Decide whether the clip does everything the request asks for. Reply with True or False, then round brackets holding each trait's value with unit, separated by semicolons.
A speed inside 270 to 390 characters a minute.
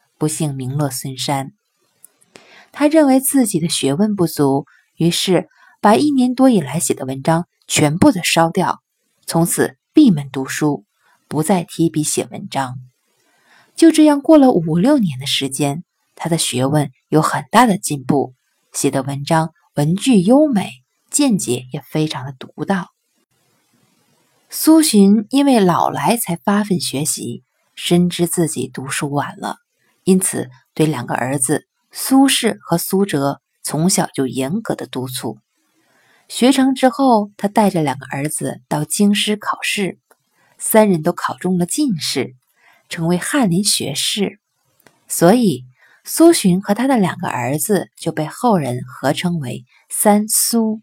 False (205 characters per minute)